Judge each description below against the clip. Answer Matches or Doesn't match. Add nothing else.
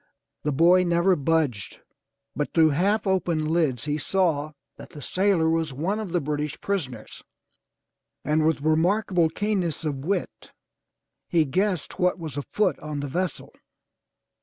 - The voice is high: Doesn't match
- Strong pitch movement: Doesn't match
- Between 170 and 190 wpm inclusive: Doesn't match